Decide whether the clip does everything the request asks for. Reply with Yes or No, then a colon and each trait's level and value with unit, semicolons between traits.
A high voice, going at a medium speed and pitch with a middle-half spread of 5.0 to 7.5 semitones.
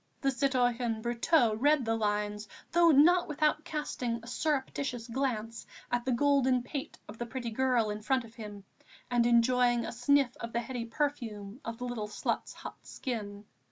No: high, 245 Hz; average, 170 wpm; average, 3.0 semitones